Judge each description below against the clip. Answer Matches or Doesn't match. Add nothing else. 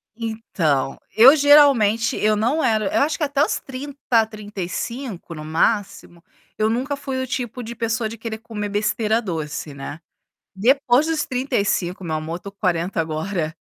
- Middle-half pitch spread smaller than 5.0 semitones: Doesn't match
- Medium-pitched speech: Doesn't match